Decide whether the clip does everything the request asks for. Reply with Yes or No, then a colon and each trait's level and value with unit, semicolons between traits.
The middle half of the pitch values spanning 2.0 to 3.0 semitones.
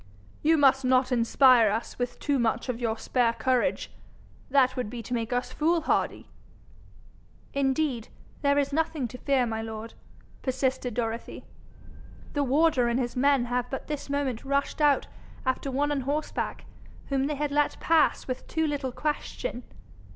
Yes: average, 2.7 semitones